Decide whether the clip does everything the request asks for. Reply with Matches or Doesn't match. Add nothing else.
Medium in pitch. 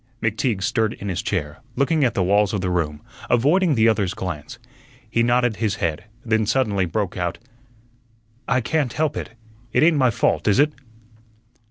Doesn't match